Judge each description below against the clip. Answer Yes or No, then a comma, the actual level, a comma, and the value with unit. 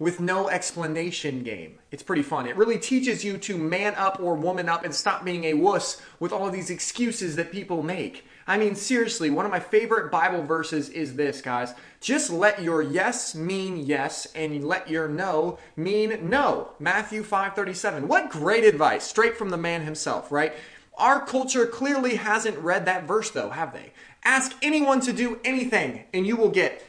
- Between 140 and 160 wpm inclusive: No, average, 185 wpm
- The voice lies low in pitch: No, medium, 185 Hz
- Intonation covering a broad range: No, average, 5.0 semitones